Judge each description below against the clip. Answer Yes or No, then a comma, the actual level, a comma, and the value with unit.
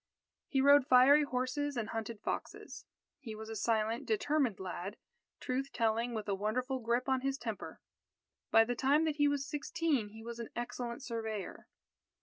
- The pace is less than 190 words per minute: Yes, average, 165 wpm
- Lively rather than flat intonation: No, average, 3.7 semitones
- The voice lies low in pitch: No, high, 245 Hz